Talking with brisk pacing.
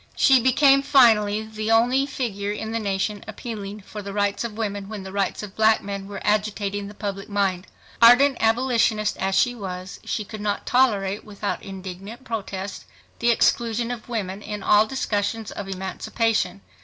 No: average, 170 wpm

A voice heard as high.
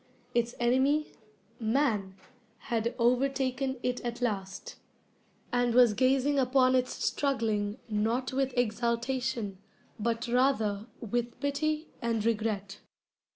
Yes: high, 240 Hz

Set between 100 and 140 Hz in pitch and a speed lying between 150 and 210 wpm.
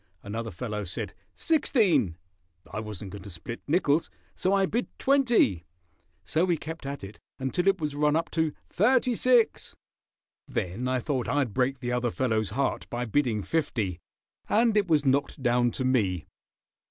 Yes: low, 135 Hz; average, 165 wpm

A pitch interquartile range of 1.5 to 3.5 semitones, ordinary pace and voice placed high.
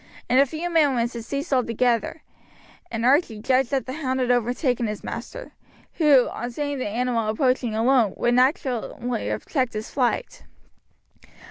Yes: average, 2.7 semitones; average, 155 wpm; very high, 250 Hz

